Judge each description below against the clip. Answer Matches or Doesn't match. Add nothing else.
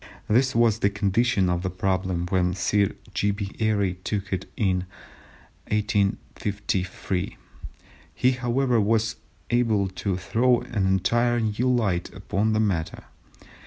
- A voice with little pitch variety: Doesn't match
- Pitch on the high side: Doesn't match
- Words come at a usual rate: Doesn't match